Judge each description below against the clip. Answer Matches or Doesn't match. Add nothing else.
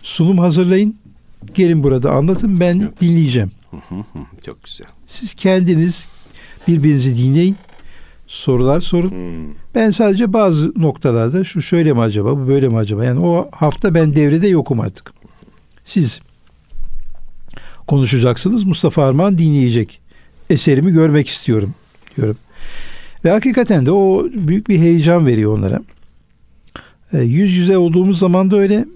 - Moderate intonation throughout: Doesn't match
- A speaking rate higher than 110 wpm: Matches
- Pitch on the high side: Doesn't match